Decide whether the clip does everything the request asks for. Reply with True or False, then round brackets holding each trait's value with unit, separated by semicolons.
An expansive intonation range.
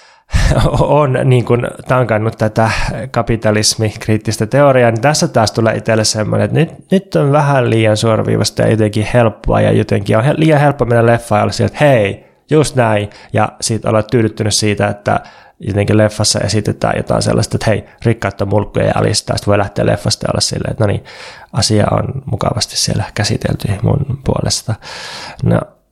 False (3.3 semitones)